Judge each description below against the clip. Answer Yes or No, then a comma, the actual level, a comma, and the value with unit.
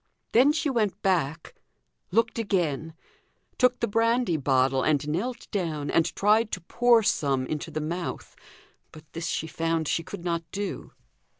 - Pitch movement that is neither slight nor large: No, wide, 6.4 semitones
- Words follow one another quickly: No, average, 155 wpm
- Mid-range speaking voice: Yes, medium, 170 Hz